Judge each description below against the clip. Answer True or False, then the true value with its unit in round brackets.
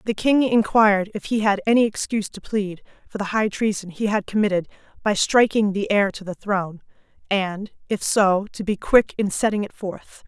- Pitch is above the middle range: True (205 Hz)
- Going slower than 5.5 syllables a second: True (5.1 syllables/s)